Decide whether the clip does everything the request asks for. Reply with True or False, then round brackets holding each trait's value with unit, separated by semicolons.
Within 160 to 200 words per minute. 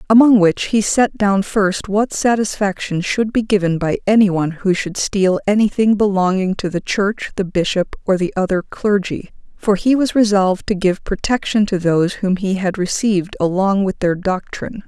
True (180 wpm)